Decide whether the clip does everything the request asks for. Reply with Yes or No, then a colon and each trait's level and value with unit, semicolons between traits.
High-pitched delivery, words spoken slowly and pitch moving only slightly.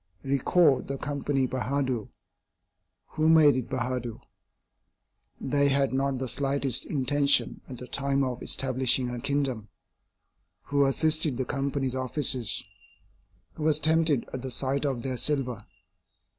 No: low, 135 Hz; slow, 130 wpm; narrow, 1.8 semitones